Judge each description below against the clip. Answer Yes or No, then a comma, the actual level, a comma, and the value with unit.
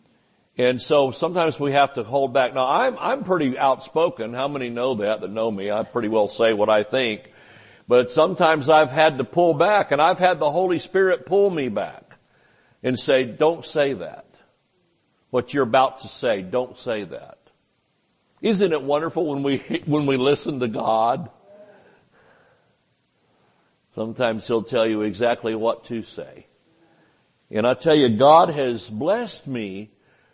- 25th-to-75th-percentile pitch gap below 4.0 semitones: No, average, 5.2 semitones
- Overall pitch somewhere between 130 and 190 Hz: Yes, low, 135 Hz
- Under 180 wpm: Yes, average, 160 wpm